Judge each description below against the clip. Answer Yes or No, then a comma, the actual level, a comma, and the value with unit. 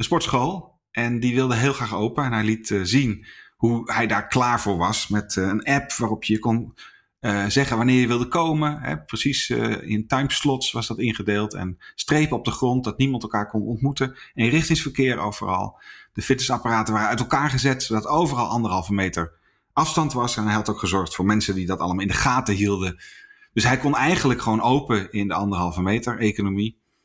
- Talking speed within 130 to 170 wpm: No, fast, 200 wpm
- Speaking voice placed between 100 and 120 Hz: Yes, low, 115 Hz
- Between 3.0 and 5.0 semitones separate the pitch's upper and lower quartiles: Yes, average, 4.1 semitones